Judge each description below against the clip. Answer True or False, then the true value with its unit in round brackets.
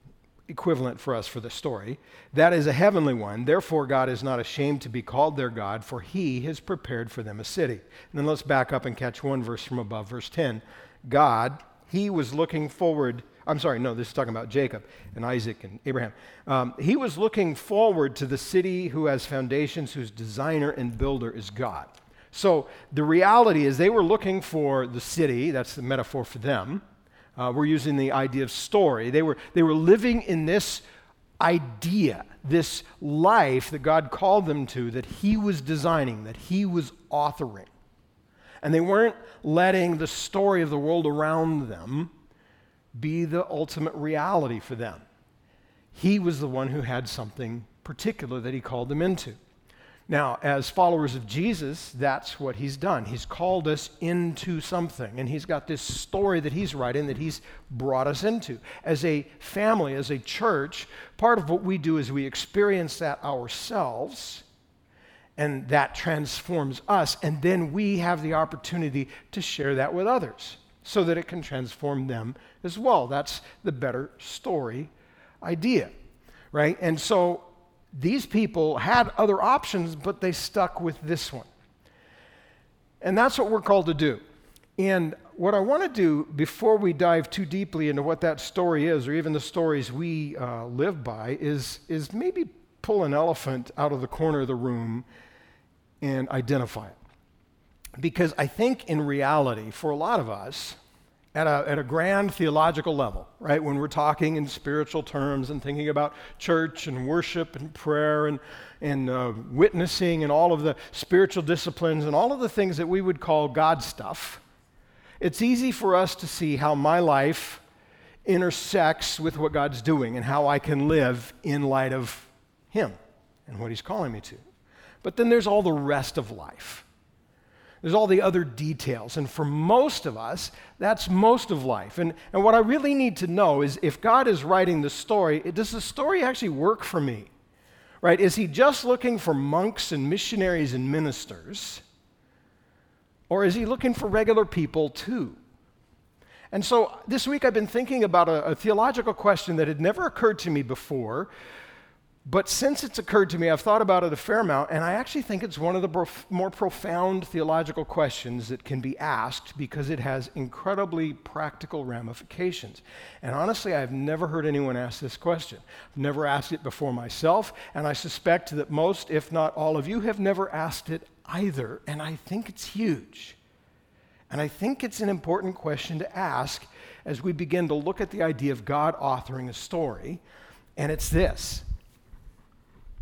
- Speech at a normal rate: True (180 wpm)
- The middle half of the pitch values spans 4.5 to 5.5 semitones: True (5.1 semitones)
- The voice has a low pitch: False (155 Hz)